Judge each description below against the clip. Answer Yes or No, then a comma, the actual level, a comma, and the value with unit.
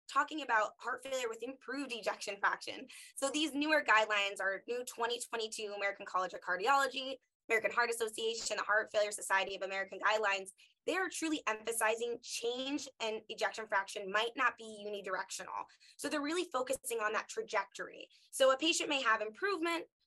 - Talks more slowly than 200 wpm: Yes, average, 160 wpm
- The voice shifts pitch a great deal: Yes, wide, 5.7 semitones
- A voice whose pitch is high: Yes, high, 235 Hz